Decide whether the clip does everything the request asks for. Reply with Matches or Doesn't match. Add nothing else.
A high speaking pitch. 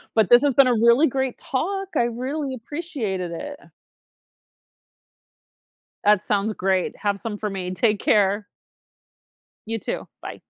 Matches